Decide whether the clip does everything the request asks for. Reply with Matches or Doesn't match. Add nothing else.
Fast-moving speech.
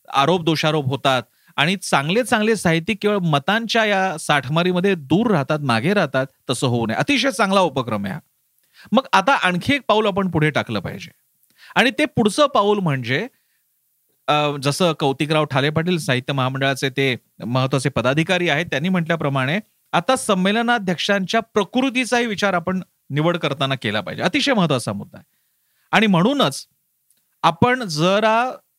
Matches